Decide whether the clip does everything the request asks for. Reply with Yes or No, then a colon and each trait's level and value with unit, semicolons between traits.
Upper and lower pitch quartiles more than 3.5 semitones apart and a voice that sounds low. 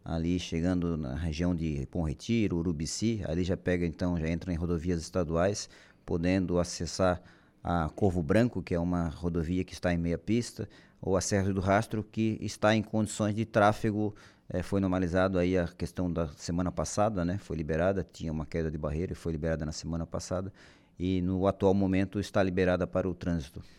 No: narrow, 2.5 semitones; very low, 90 Hz